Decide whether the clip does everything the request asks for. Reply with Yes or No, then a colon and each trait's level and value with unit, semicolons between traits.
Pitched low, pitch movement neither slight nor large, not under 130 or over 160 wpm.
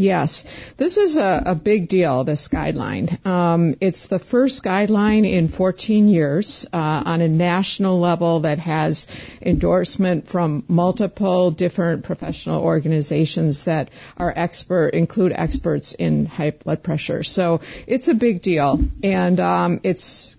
No: medium, 175 Hz; average, 3.2 semitones; average, 140 wpm